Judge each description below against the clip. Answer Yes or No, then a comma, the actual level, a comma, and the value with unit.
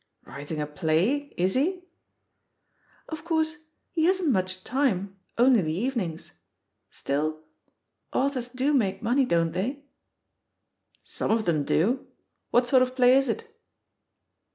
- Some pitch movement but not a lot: No, wide, 7.6 semitones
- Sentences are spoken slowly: Yes, slow, 130 wpm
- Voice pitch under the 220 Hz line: No, high, 245 Hz